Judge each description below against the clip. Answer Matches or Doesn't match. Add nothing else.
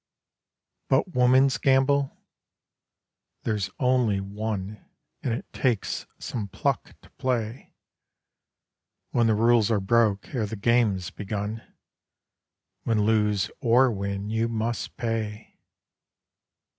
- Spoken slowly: Matches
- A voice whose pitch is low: Matches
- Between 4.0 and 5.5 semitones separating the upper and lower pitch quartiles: Doesn't match